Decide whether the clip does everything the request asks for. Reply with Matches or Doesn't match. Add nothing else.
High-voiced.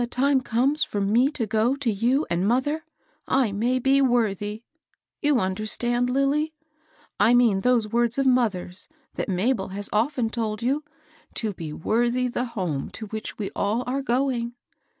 Matches